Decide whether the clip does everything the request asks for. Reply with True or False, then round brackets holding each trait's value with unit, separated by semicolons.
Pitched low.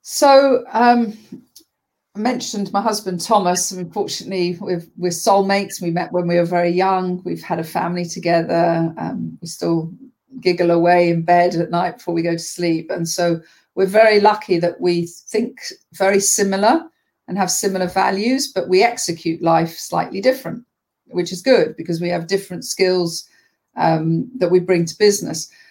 False (185 Hz)